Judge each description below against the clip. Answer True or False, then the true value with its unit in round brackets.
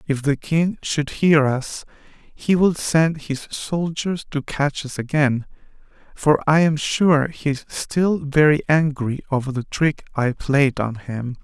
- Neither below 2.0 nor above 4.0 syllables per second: True (3.7 syllables/s)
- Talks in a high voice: False (145 Hz)